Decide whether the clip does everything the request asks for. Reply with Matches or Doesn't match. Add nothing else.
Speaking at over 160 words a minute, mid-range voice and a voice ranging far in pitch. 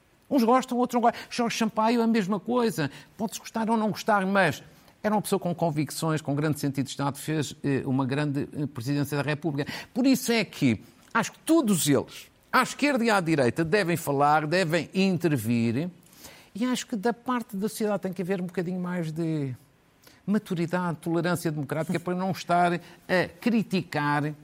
Matches